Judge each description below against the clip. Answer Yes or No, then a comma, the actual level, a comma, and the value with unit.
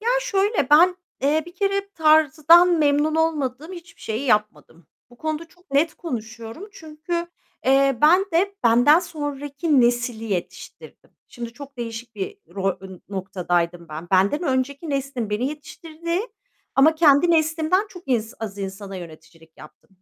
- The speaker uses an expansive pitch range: Yes, wide, 6.6 semitones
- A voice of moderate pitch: No, very high, 280 Hz